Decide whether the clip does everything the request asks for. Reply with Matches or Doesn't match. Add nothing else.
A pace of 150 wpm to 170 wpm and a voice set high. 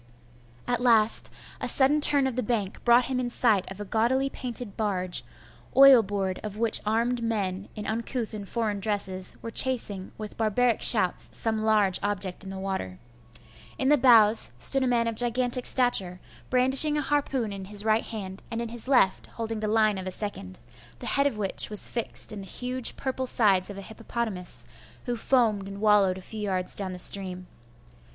Doesn't match